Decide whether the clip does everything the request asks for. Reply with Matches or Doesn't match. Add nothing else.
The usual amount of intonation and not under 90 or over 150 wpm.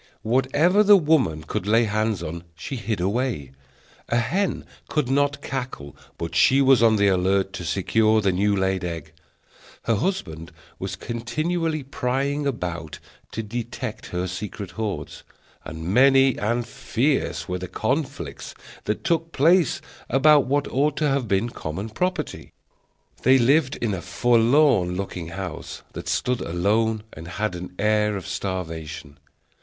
Doesn't match